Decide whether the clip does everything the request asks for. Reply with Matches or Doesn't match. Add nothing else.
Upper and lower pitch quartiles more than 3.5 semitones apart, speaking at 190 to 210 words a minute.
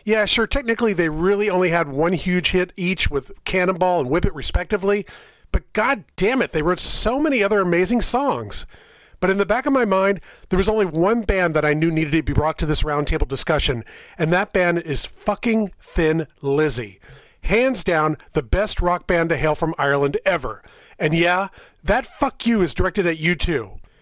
Matches